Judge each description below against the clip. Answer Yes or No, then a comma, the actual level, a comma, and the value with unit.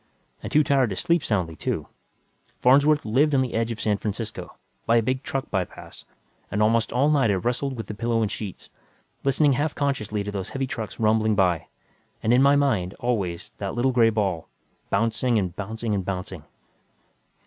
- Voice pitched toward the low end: Yes, low, 115 Hz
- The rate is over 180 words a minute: Yes, average, 190 wpm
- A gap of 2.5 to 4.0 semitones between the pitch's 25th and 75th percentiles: No, average, 4.5 semitones